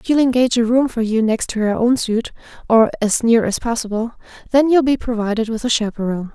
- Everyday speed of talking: No, fast, 215 wpm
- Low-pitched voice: No, high, 230 Hz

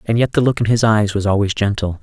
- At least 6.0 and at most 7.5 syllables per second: Yes, 6.2 syllables/s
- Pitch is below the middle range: Yes, low, 105 Hz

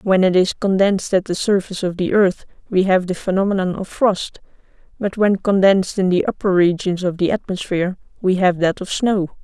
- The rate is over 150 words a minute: Yes, average, 195 wpm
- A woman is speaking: Yes, female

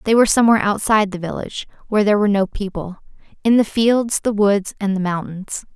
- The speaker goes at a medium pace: Yes, average, 190 wpm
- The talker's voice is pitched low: No, high, 205 Hz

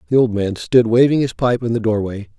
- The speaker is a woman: No, male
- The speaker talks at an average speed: No, fast, 250 wpm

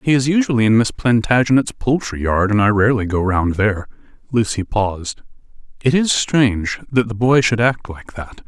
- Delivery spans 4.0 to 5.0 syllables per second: No, 5.2 syllables/s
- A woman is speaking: No, male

